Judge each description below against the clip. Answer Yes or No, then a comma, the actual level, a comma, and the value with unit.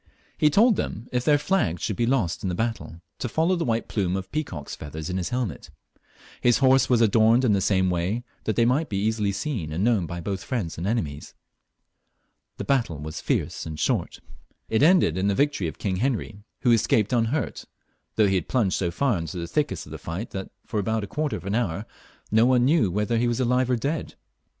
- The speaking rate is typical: No, fast, 220 wpm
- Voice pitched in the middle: No, low, 110 Hz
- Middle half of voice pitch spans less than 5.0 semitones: No, average, 5.3 semitones